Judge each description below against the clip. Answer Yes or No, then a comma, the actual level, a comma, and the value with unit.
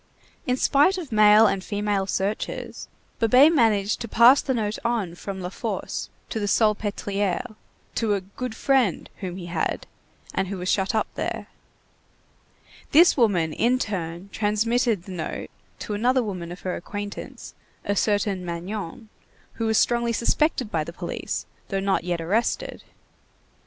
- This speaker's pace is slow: No, average, 150 wpm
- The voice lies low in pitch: No, high, 210 Hz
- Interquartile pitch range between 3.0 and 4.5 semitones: Yes, average, 3.6 semitones